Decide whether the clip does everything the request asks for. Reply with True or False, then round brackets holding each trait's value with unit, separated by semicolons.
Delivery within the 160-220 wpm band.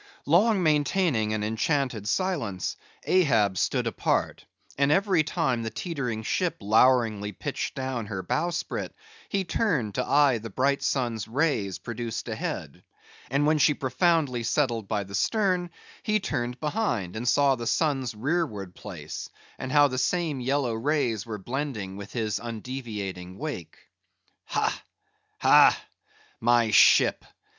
False (135 wpm)